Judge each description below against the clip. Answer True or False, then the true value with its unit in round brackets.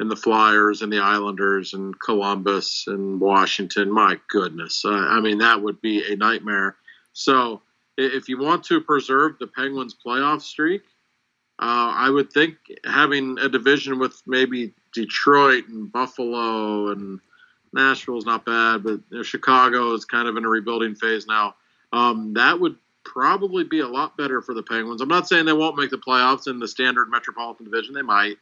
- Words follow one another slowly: False (175 wpm)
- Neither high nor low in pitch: False (120 Hz)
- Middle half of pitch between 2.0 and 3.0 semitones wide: False (3.8 semitones)